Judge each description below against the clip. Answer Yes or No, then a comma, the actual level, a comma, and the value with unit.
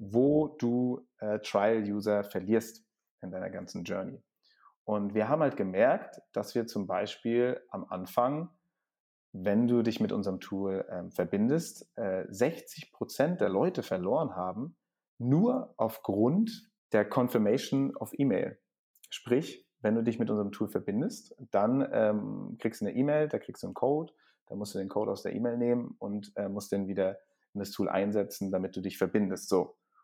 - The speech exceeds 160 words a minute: Yes, average, 170 wpm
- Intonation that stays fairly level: No, average, 3.8 semitones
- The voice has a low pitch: Yes, low, 105 Hz